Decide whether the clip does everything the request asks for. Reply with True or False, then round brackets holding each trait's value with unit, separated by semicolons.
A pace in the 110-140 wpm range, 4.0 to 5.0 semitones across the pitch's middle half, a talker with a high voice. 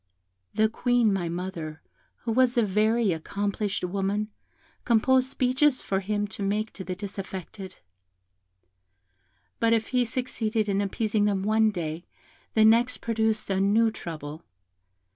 False (135 wpm; 2.9 semitones; 210 Hz)